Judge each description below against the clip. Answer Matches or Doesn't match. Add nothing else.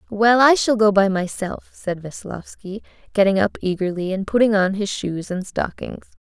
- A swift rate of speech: Doesn't match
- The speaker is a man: Doesn't match